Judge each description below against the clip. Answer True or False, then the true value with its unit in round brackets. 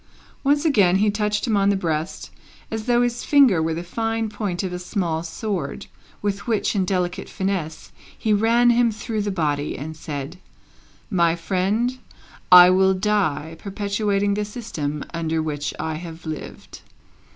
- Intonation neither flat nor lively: True (4.6 semitones)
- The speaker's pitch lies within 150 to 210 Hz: True (190 Hz)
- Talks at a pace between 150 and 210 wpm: True (160 wpm)